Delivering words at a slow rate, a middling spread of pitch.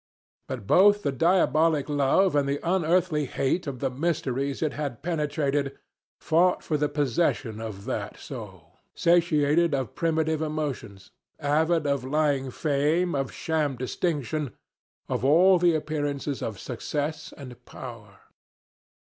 Yes: slow, 130 wpm; average, 3.3 semitones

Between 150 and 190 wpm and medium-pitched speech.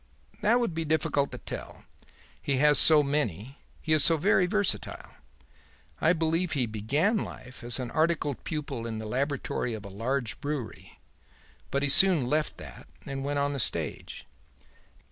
Yes: average, 165 wpm; medium, 145 Hz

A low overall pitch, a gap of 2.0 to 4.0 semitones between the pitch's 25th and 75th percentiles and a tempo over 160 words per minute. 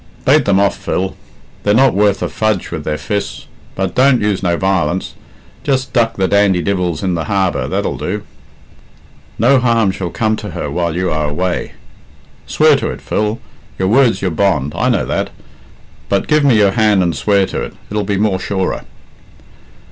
Yes: low, 100 Hz; average, 3.0 semitones; average, 185 wpm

